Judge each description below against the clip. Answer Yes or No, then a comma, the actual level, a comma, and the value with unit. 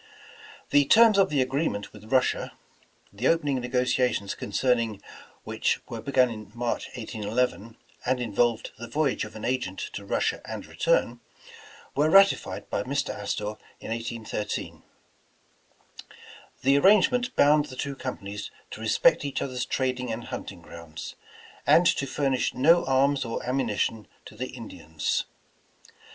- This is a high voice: No, low, 125 Hz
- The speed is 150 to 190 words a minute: No, average, 140 wpm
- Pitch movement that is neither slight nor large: Yes, average, 3.9 semitones